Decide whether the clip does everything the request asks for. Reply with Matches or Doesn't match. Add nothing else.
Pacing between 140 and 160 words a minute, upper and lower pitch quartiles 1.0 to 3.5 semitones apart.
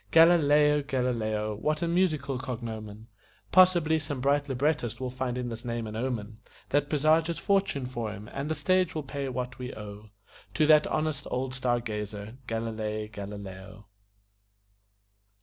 Doesn't match